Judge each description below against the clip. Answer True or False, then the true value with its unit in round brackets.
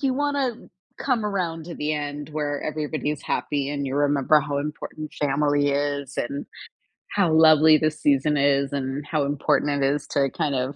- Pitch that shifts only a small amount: True (1.6 semitones)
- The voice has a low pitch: False (145 Hz)